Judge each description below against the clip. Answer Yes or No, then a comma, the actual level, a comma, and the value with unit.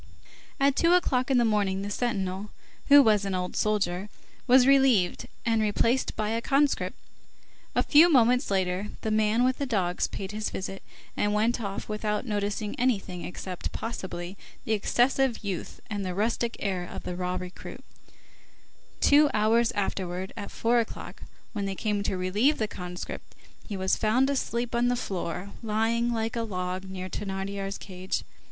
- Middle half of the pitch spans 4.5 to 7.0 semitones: No, average, 3.8 semitones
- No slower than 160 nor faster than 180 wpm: Yes, average, 165 wpm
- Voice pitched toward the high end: Yes, high, 210 Hz